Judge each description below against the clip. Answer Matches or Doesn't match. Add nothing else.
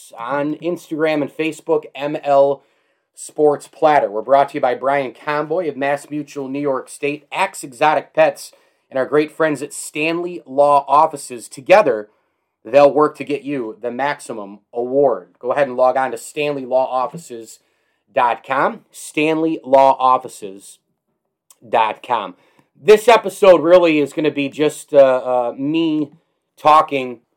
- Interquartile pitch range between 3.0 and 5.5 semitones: Doesn't match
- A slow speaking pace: Matches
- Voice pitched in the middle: Matches